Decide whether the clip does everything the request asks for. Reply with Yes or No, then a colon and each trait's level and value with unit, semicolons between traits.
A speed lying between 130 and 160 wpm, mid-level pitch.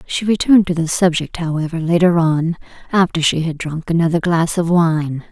No: average, 180 wpm; medium, 170 Hz